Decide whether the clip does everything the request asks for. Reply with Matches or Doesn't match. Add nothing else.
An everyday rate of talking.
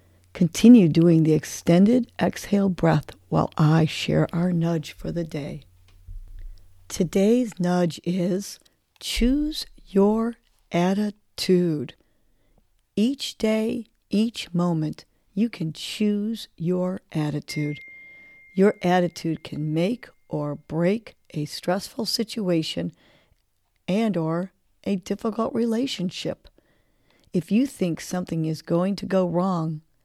Doesn't match